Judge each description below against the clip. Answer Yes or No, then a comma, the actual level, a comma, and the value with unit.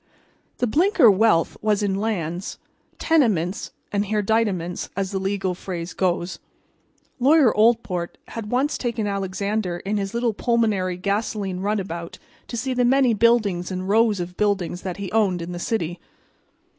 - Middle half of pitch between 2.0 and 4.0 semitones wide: Yes, average, 3.7 semitones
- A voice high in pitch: Yes, high, 200 Hz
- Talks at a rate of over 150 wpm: No, average, 145 wpm